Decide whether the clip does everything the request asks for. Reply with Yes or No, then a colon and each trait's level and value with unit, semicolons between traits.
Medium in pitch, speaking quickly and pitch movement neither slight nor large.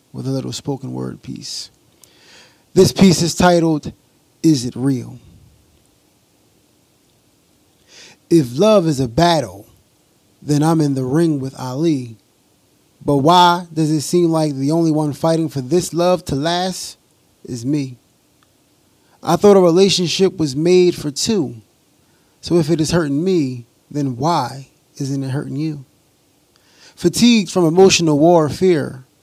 No: medium, 155 Hz; slow, 135 wpm; average, 4.2 semitones